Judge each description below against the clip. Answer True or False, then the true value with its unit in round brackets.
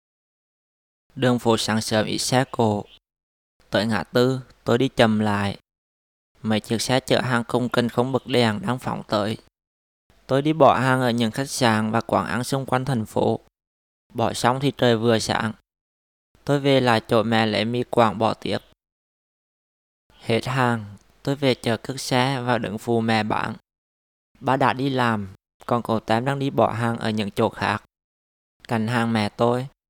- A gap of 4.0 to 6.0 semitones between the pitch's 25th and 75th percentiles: False (2.8 semitones)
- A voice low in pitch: True (115 Hz)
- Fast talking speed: False (180 wpm)